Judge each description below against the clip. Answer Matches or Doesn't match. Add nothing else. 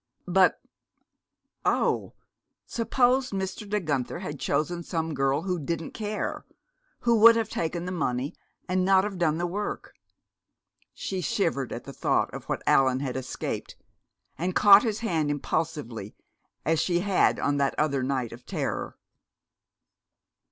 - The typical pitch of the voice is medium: Matches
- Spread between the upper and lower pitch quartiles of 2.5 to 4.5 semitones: Doesn't match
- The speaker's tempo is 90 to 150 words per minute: Matches